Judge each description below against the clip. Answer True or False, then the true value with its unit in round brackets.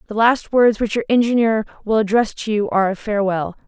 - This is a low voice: False (215 Hz)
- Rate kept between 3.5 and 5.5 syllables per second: False (6.0 syllables/s)